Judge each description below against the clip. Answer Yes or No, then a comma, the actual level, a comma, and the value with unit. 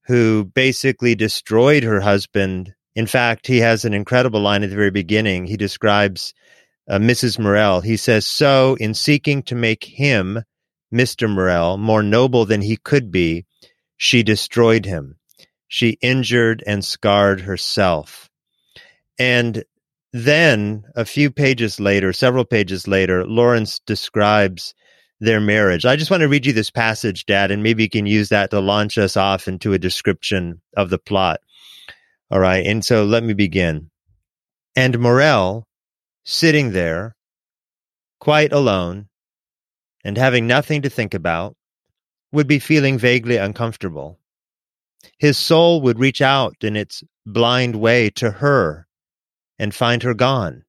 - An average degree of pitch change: Yes, average, 3.9 semitones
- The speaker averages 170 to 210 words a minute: No, average, 145 wpm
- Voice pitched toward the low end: Yes, low, 110 Hz